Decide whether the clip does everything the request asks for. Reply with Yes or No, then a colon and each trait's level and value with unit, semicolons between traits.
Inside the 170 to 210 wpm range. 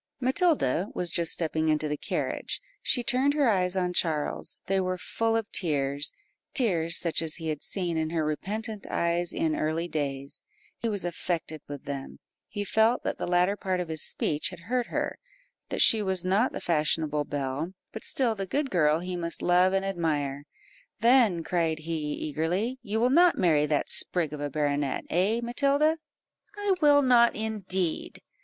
Yes: average, 175 wpm